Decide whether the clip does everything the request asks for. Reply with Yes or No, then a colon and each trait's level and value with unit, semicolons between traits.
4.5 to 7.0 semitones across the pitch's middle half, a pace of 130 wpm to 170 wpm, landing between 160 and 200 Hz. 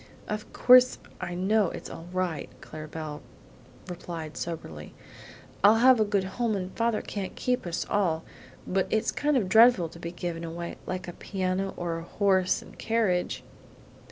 No: average, 4.1 semitones; average, 165 wpm; medium, 185 Hz